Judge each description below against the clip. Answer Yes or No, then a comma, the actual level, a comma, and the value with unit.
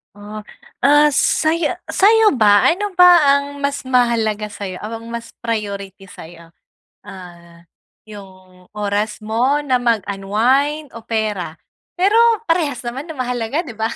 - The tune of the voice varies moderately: No, wide, 5.8 semitones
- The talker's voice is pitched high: Yes, high, 230 Hz